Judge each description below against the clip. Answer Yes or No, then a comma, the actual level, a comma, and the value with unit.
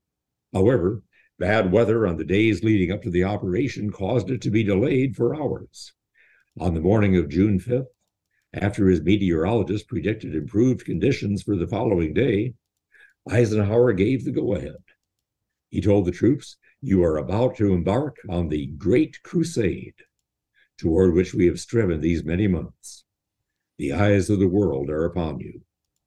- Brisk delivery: No, average, 155 wpm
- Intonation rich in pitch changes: No, average, 3.8 semitones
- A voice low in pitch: Yes, low, 100 Hz